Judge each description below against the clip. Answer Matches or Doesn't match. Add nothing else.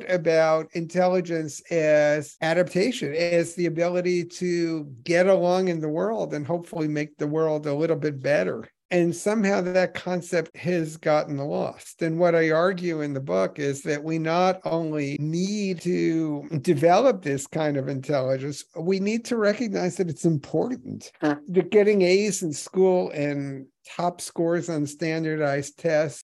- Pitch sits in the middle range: Matches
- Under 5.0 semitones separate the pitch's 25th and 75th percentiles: Matches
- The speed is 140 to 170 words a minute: Matches